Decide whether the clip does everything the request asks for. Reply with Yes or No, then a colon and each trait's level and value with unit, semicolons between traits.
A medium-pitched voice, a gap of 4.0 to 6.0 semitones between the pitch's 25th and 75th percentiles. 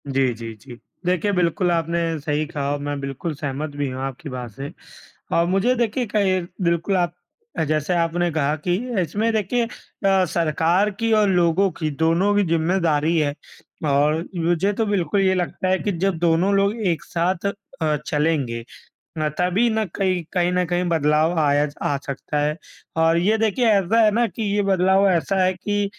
Yes: medium, 170 Hz; average, 4.3 semitones